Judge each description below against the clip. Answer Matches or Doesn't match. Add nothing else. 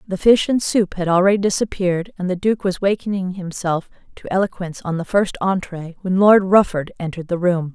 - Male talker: Doesn't match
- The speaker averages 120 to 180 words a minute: Doesn't match